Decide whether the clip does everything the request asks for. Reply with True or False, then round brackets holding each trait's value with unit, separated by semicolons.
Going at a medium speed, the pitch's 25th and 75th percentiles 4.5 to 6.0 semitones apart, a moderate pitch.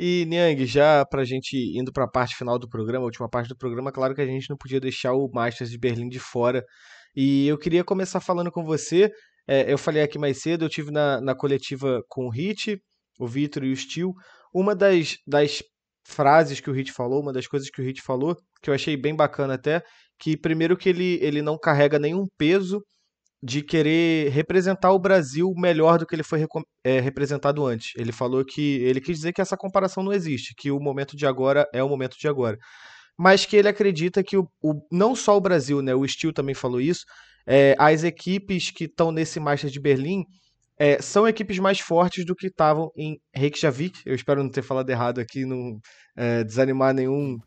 False (210 wpm; 4.8 semitones; 145 Hz)